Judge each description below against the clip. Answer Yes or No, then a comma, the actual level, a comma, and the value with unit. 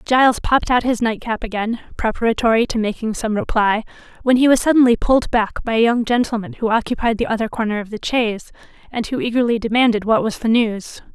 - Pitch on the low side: No, high, 230 Hz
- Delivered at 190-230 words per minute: Yes, average, 200 wpm